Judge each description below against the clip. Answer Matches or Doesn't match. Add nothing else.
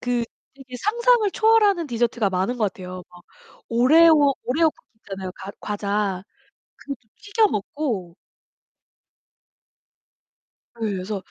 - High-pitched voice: Matches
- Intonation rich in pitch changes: Matches